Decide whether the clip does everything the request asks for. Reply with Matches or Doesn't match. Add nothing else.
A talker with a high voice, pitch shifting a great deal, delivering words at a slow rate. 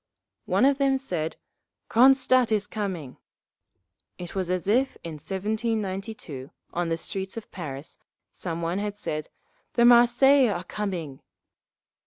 Matches